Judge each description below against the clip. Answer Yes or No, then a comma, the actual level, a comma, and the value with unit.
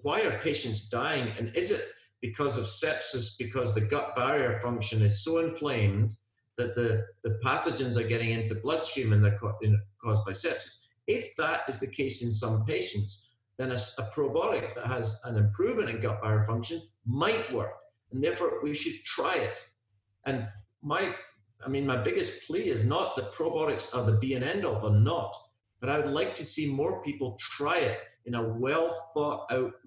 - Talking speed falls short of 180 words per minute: No, average, 190 wpm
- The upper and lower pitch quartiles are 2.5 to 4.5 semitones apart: No, average, 5.1 semitones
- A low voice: Yes, low, 120 Hz